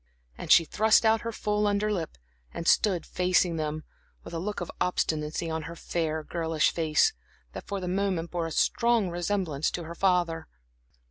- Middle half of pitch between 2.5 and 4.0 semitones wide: Yes, average, 3.7 semitones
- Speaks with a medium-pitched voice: Yes, medium, 175 Hz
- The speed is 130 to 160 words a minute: No, average, 180 wpm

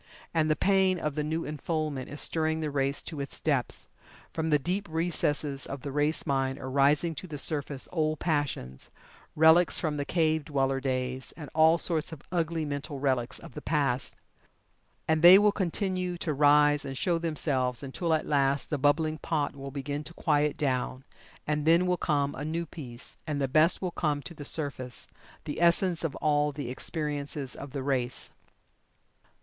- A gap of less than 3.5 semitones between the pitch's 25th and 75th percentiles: Yes, average, 2.7 semitones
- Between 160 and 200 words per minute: Yes, average, 180 wpm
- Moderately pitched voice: Yes, medium, 150 Hz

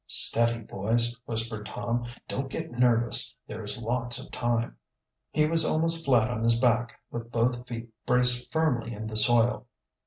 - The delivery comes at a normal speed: Yes, average, 160 wpm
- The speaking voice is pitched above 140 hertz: No, low, 120 Hz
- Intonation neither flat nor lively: No, narrow, 1.4 semitones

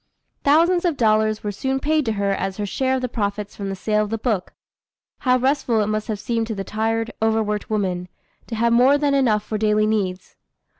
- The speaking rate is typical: No, fast, 220 wpm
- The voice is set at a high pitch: Yes, high, 220 Hz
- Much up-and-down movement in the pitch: No, average, 3.4 semitones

